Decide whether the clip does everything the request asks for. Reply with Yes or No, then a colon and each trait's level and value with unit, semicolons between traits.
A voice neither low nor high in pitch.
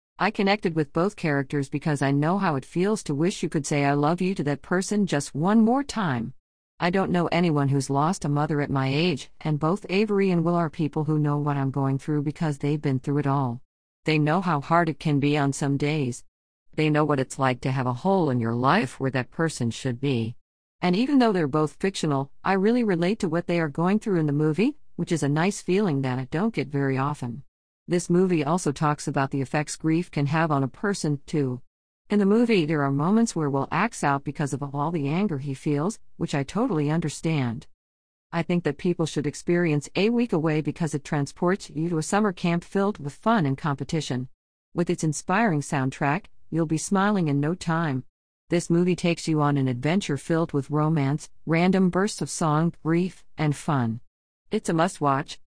Yes: medium, 155 Hz